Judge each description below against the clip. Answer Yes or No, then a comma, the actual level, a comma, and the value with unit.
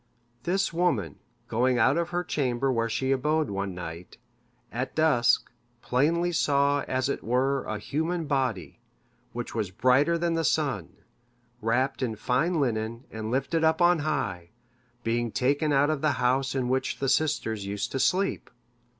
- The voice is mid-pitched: No, low, 130 Hz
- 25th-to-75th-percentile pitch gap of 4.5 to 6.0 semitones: Yes, average, 5.1 semitones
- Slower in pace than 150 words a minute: No, average, 160 wpm